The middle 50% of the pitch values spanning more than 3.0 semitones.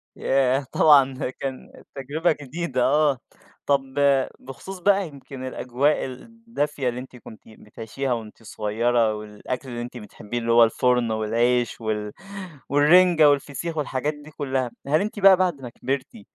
Yes: average, 3.9 semitones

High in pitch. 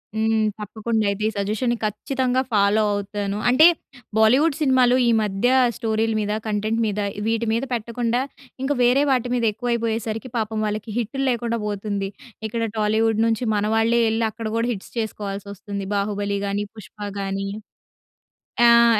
Yes: high, 220 Hz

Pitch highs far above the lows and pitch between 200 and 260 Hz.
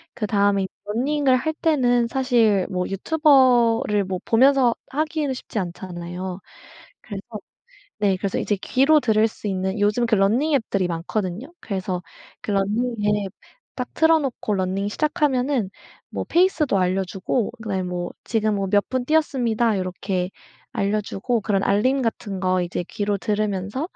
No: average, 4.9 semitones; high, 210 Hz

